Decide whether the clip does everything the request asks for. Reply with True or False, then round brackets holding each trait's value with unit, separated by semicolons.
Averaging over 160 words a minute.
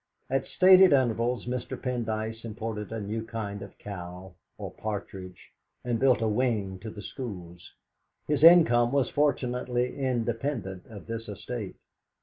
False (135 wpm)